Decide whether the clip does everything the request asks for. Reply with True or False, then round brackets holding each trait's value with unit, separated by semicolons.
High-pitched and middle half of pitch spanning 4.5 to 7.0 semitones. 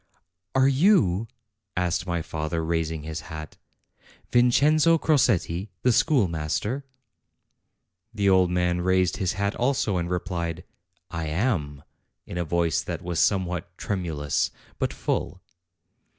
False (90 Hz; 5.0 semitones)